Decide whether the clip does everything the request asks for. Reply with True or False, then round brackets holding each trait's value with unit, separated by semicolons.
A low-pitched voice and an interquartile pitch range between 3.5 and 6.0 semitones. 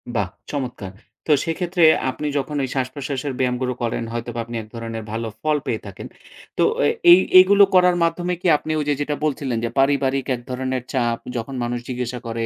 True (130 Hz; 4.0 semitones)